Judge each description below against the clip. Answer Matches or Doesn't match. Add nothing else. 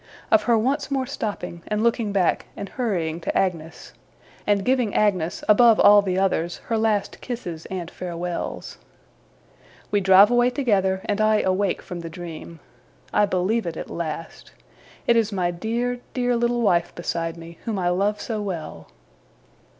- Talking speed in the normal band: Matches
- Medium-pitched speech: Doesn't match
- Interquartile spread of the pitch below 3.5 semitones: Doesn't match